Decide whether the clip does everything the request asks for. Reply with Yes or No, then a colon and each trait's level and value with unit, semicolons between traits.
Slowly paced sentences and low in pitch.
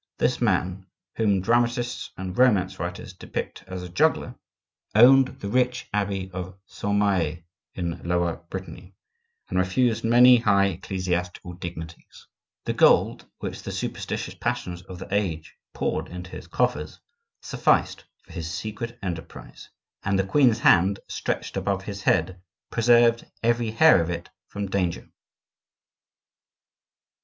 Yes: slow, 130 wpm; very low, 95 Hz